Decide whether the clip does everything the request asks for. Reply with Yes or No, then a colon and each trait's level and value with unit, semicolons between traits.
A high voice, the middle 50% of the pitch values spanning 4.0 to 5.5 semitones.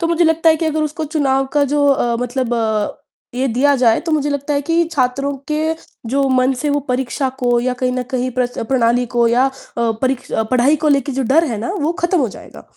No: very high, 270 Hz; average, 3.4 semitones